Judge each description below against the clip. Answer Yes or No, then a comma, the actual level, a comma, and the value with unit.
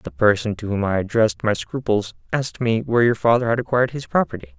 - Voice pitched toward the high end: No, low, 110 Hz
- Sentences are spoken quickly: Yes, fast, 220 wpm